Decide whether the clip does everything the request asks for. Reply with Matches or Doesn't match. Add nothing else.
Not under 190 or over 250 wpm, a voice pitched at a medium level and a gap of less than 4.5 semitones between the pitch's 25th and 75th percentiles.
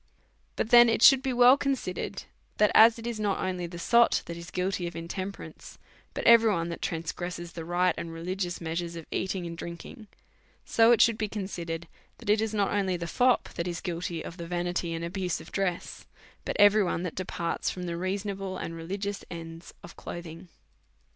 Matches